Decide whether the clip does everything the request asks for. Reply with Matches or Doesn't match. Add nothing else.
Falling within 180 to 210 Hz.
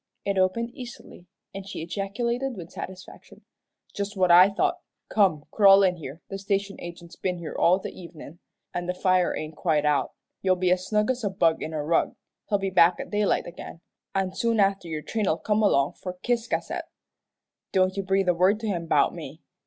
Matches